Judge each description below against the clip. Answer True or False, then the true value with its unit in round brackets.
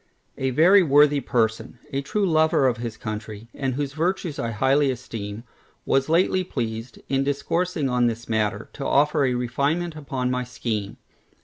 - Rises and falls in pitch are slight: False (4.3 semitones)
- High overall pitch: False (135 Hz)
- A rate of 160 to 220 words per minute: True (165 wpm)